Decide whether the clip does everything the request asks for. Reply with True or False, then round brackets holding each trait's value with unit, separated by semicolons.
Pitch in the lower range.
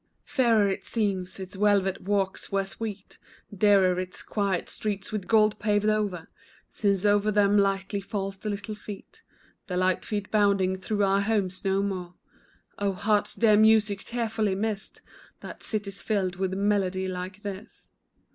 False (200 Hz)